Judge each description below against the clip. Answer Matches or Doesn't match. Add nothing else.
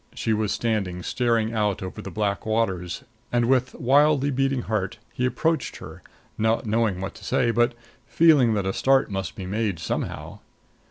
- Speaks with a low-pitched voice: Matches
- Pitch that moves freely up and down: Doesn't match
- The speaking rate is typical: Matches